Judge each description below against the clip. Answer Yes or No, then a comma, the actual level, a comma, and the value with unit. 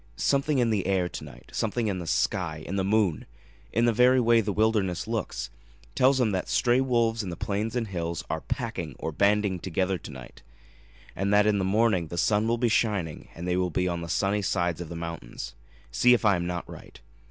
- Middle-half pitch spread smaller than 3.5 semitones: No, average, 4.5 semitones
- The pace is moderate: No, fast, 220 wpm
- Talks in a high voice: No, low, 100 Hz